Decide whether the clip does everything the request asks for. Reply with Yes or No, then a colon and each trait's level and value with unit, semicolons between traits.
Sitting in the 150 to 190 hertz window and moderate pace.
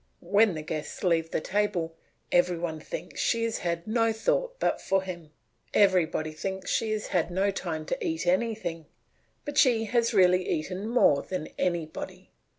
Yes: medium, 185 Hz; average, 165 wpm